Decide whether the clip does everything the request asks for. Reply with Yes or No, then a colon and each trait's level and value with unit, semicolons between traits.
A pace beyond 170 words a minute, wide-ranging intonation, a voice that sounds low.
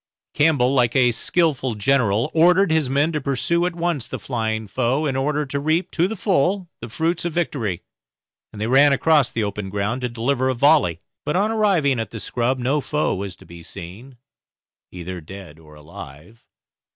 Yes: average, 190 wpm; wide, 6.3 semitones; low, 130 Hz